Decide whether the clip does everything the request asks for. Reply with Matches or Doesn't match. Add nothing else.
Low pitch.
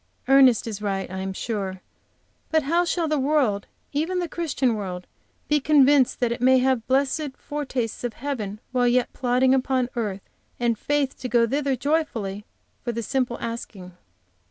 Doesn't match